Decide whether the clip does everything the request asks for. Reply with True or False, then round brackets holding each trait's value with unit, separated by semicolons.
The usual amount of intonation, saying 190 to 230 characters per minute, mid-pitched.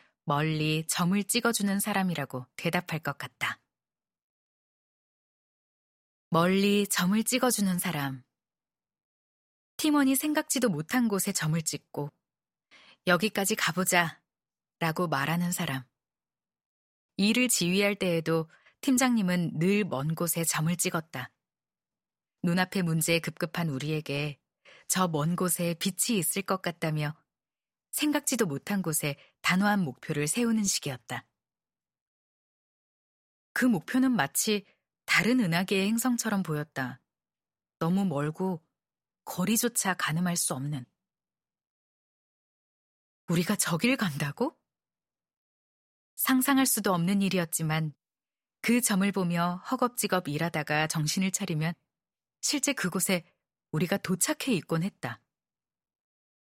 True (4.4 semitones; 225 characters per minute; 180 Hz)